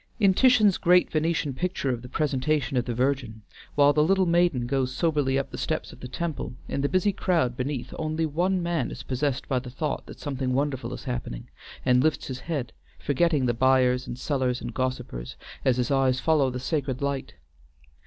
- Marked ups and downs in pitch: No, average, 3.7 semitones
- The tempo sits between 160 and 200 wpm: Yes, average, 195 wpm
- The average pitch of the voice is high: No, low, 135 Hz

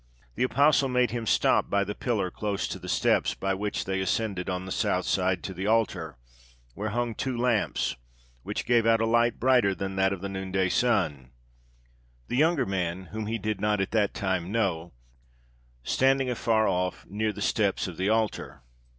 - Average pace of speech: Yes, average, 185 wpm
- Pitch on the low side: Yes, low, 105 Hz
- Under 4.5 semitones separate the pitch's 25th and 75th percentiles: Yes, average, 3.4 semitones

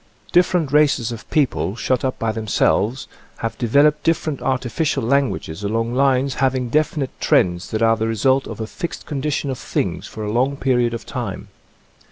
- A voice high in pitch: No, low, 130 Hz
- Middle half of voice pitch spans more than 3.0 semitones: Yes, average, 3.8 semitones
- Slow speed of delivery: No, average, 170 wpm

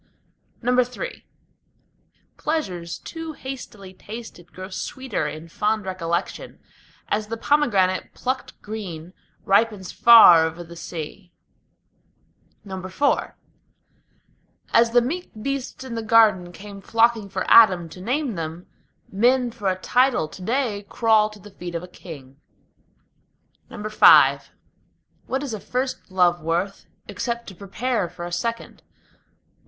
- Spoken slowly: Yes, slow, 125 wpm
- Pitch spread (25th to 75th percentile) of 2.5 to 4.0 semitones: No, average, 4.9 semitones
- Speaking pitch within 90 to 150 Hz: No, high, 205 Hz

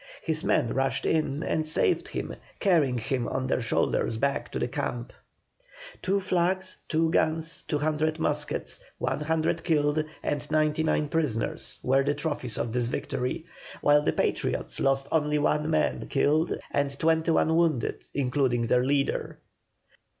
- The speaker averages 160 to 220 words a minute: No, average, 150 wpm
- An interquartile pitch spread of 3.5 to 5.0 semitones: No, average, 2.8 semitones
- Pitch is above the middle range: No, medium, 150 Hz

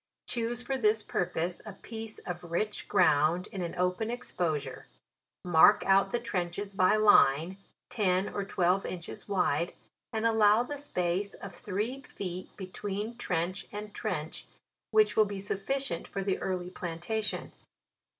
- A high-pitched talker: Yes, high, 195 Hz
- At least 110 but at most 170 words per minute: Yes, average, 145 wpm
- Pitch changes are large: No, average, 3.3 semitones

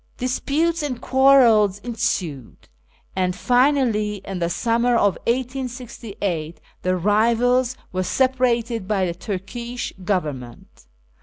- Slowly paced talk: Yes, slow, 100 wpm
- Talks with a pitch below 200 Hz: No, high, 230 Hz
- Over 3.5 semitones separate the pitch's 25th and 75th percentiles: Yes, average, 5.1 semitones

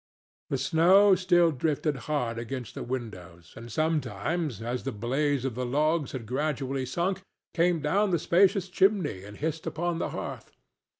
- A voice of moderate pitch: Yes, medium, 145 Hz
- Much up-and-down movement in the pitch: Yes, wide, 5.7 semitones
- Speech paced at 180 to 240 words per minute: No, average, 160 wpm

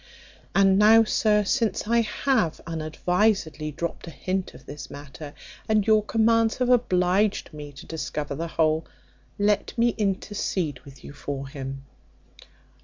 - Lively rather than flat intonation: Yes, wide, 6.0 semitones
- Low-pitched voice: No, medium, 185 Hz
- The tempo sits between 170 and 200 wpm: No, average, 140 wpm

